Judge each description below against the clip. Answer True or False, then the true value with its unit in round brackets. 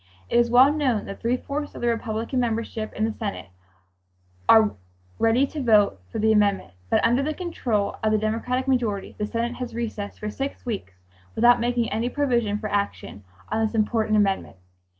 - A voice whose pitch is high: True (225 Hz)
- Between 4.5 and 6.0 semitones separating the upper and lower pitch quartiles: False (2.6 semitones)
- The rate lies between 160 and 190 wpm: True (185 wpm)